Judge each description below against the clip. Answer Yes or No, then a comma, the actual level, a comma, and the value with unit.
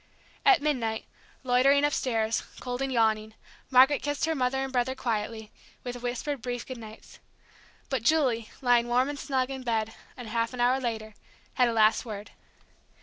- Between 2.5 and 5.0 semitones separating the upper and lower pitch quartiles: Yes, average, 2.9 semitones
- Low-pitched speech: No, high, 245 Hz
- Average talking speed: Yes, average, 160 wpm